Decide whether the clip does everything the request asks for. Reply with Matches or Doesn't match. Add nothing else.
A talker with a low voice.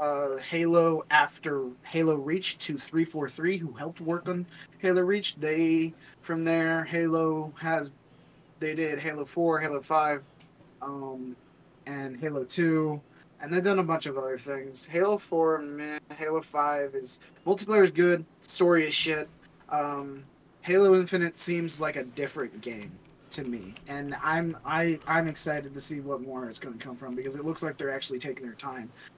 Doesn't match